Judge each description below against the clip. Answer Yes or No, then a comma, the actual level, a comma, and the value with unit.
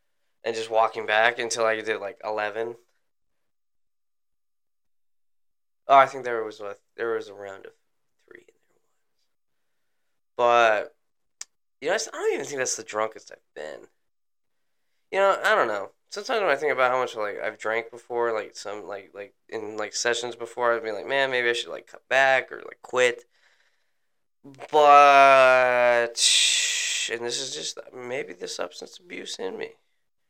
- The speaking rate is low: No, average, 165 wpm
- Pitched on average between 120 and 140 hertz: Yes, low, 135 Hz